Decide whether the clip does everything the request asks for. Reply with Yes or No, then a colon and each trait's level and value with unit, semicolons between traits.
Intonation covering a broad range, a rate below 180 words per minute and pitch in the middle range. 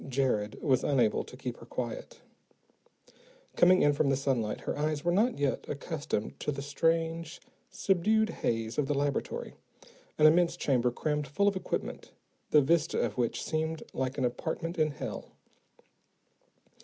No: average, 4.2 semitones; average, 155 wpm; medium, 145 Hz